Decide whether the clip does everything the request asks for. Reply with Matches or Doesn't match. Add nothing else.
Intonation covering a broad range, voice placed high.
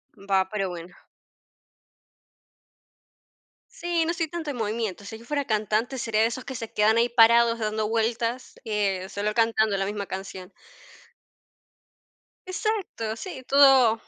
Doesn't match